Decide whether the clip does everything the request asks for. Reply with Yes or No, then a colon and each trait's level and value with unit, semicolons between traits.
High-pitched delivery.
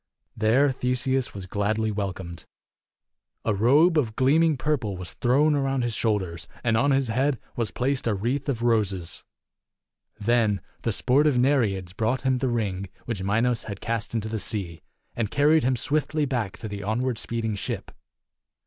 No: low, 115 Hz